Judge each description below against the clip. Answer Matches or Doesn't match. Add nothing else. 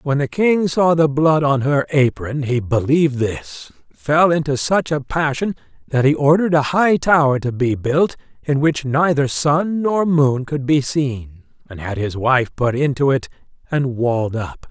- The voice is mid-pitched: Matches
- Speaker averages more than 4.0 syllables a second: Matches